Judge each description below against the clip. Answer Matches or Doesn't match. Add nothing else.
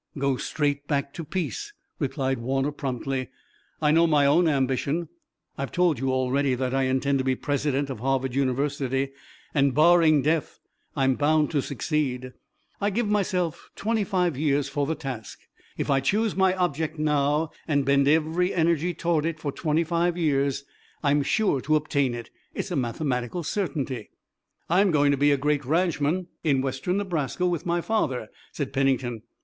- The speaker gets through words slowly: Doesn't match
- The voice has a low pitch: Doesn't match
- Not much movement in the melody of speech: Doesn't match